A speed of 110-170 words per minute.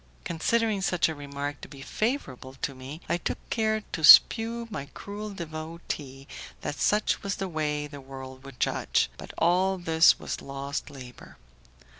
Yes: average, 160 wpm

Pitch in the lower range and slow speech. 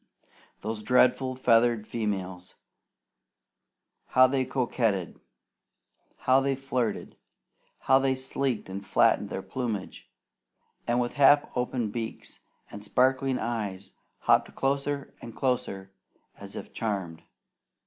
Yes: low, 120 Hz; slow, 105 wpm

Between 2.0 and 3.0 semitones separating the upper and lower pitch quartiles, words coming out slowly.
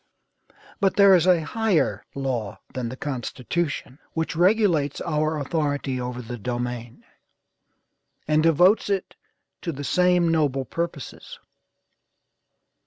No: average, 5.2 semitones; slow, 110 wpm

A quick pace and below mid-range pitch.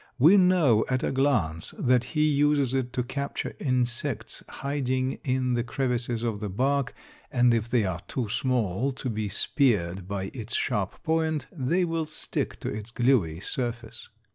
No: average, 165 wpm; low, 125 Hz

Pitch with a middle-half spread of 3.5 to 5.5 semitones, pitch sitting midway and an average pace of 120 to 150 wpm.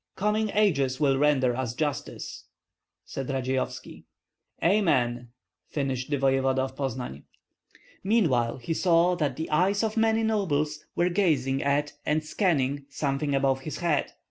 Yes: average, 4.7 semitones; medium, 145 Hz; slow, 135 wpm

